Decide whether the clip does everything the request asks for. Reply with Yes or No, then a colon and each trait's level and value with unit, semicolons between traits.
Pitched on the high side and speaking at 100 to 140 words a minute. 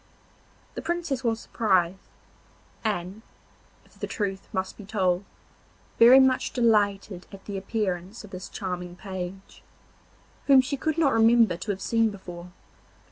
Yes: high, 200 Hz; slow, 135 wpm